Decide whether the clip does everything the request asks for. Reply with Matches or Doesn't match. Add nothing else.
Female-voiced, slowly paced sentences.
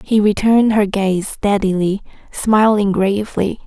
Matches